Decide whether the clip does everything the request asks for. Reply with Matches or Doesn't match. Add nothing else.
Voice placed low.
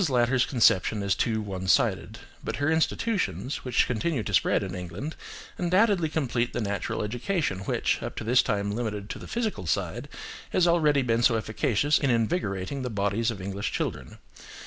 Matches